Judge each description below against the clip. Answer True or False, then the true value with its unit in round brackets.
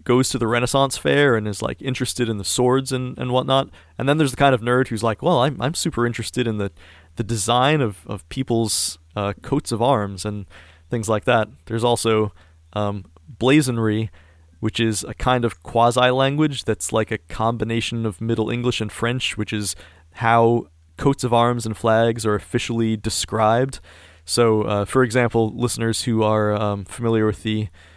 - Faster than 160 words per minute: True (185 wpm)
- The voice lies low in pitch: True (115 Hz)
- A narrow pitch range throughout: False (3.0 semitones)